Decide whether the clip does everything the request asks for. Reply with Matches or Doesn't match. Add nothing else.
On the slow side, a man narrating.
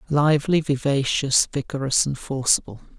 Matches